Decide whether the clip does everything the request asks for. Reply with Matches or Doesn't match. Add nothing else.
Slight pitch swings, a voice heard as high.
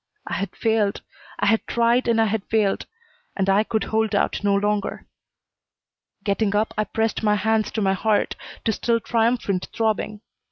Matches